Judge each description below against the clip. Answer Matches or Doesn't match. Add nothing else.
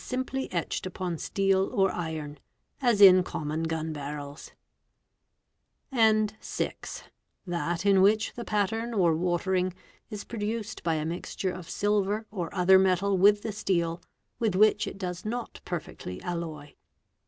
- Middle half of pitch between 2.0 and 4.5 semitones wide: Matches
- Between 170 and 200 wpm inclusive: Doesn't match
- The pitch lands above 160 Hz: Matches